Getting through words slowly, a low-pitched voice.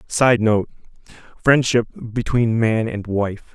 Yes: slow, 100 wpm; low, 115 Hz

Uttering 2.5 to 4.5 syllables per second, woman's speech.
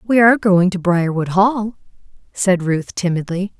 Yes: 4.4 syllables/s; female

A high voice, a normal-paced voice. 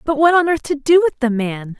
No: very high, 285 Hz; fast, 300 wpm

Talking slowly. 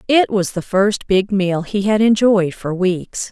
No: average, 200 wpm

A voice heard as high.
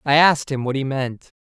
No: medium, 140 Hz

